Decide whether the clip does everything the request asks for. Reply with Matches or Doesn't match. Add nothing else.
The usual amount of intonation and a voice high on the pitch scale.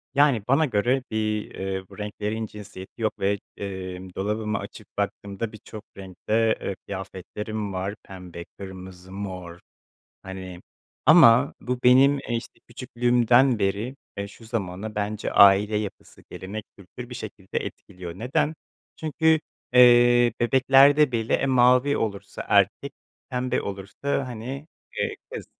Doesn't match